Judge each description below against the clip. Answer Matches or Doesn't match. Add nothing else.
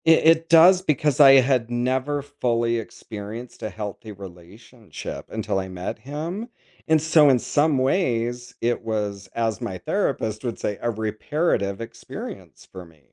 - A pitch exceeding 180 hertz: Doesn't match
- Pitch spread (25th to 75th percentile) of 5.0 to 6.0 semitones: Matches